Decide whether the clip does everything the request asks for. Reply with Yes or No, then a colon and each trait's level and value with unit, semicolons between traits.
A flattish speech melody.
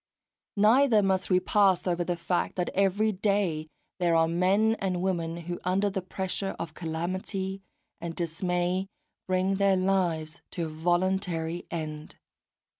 Yes: narrow, 2.3 semitones